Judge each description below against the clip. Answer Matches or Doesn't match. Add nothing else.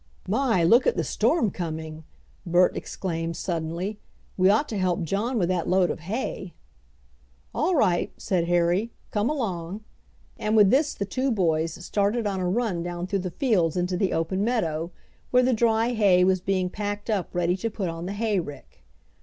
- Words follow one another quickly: Doesn't match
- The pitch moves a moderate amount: Matches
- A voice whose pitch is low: Doesn't match